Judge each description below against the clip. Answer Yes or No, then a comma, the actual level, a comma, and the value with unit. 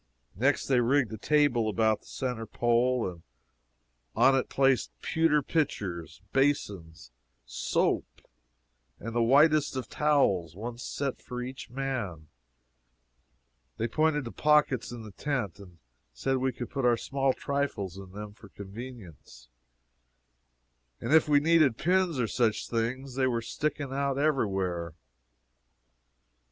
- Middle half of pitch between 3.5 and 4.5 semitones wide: No, average, 5.2 semitones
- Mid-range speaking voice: No, low, 125 Hz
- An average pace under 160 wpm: Yes, slow, 135 wpm